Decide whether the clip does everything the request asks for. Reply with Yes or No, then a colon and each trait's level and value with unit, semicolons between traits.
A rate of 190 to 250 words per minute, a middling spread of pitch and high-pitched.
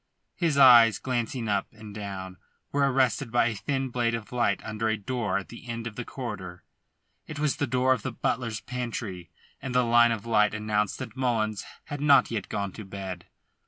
No: average, 195 wpm; average, 3.3 semitones; low, 115 Hz